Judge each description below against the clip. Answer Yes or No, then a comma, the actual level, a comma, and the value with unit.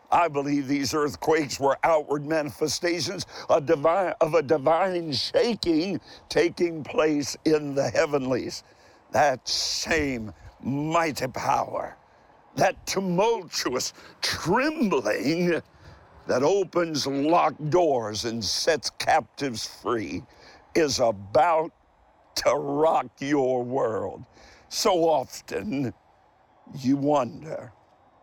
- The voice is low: No, medium, 150 Hz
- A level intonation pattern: No, average, 3.8 semitones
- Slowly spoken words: Yes, slow, 85 wpm